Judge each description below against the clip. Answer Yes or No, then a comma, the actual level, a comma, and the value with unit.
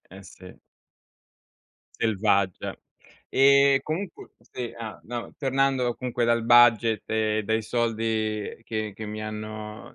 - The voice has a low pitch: Yes, low, 110 Hz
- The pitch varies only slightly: Yes, narrow, 2.1 semitones